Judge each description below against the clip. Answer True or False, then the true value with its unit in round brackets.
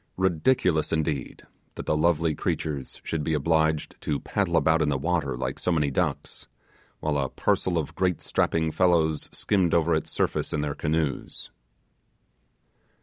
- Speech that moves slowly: False (150 wpm)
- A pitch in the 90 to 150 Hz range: False (80 Hz)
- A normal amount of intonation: False (2.2 semitones)